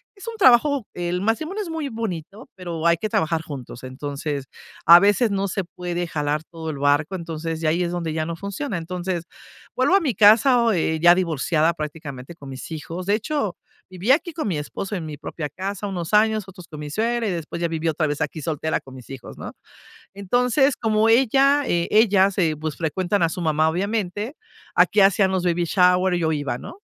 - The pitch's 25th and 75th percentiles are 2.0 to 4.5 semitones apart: No, average, 5.1 semitones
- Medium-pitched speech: Yes, medium, 175 Hz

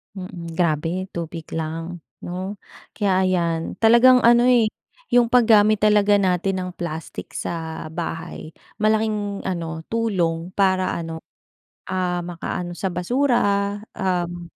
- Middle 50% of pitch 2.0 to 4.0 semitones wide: Yes, average, 3.7 semitones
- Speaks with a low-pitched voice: No, medium, 185 Hz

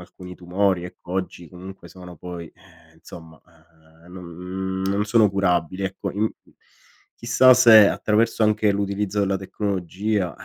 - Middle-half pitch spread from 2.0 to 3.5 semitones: Yes, narrow, 2.6 semitones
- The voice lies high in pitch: No, very low, 95 Hz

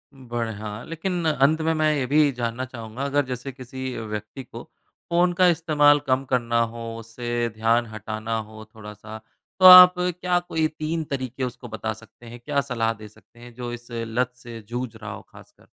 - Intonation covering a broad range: No, average, 4.4 semitones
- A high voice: No, low, 120 Hz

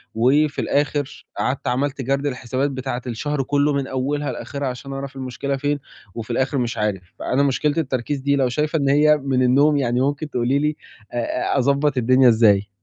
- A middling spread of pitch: No, narrow, 2.3 semitones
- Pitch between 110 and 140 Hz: Yes, low, 135 Hz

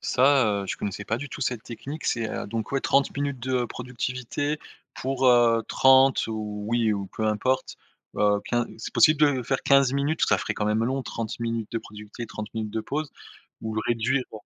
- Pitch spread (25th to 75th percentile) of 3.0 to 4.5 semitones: Yes, average, 3.5 semitones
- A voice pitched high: No, low, 120 Hz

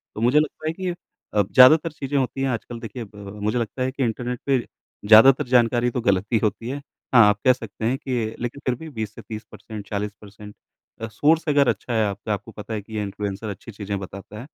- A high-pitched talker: No, low, 115 Hz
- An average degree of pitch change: Yes, average, 3.7 semitones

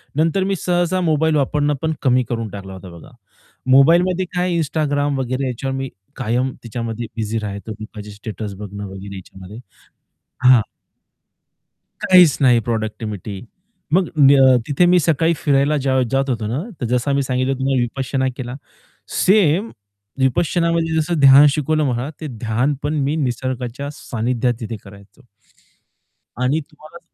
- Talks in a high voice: No, low, 130 Hz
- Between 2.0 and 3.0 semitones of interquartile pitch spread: No, average, 4.9 semitones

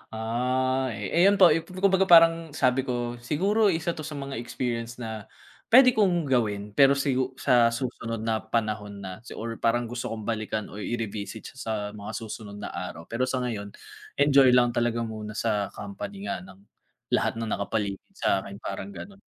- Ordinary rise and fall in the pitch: Yes, average, 4.6 semitones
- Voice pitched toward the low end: Yes, low, 120 Hz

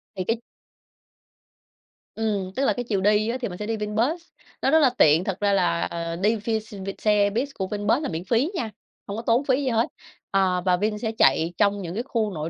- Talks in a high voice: Yes, high, 210 Hz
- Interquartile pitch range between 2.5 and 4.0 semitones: Yes, average, 3.6 semitones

